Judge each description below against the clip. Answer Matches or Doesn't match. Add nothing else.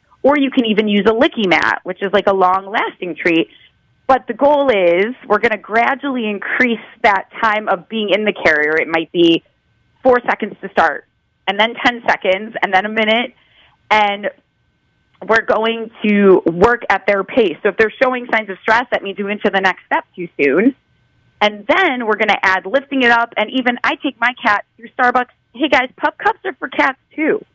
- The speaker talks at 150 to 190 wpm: Doesn't match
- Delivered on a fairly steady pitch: Doesn't match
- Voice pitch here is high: Matches